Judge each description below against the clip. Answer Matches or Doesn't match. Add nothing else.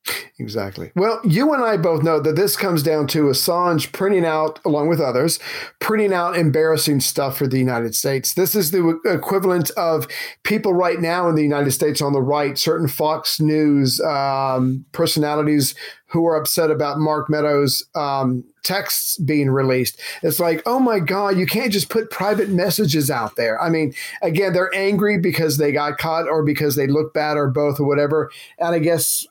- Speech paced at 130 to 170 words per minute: Doesn't match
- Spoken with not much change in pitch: Doesn't match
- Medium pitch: Matches